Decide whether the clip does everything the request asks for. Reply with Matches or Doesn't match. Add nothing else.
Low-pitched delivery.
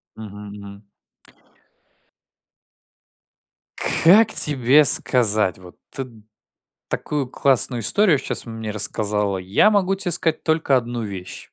Matches